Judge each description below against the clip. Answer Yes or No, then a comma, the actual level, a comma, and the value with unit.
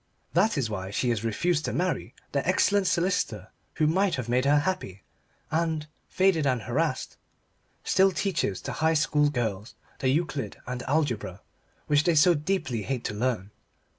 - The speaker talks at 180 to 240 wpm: No, average, 165 wpm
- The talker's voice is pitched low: No, medium, 145 Hz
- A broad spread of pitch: Yes, wide, 6.3 semitones